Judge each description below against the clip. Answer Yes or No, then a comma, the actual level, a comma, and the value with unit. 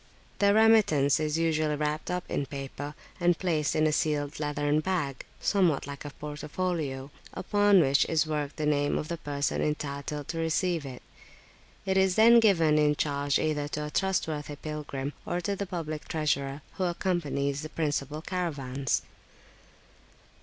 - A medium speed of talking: Yes, average, 155 wpm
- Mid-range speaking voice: Yes, medium, 150 Hz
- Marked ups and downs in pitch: No, average, 3.2 semitones